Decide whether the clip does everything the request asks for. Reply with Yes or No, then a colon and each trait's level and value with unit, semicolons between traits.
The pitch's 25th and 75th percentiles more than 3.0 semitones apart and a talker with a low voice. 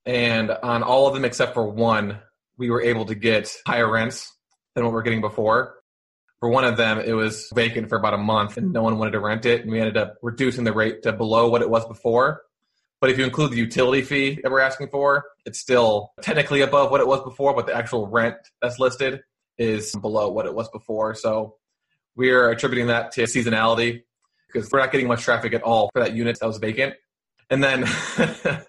No: narrow, 2.5 semitones; low, 115 Hz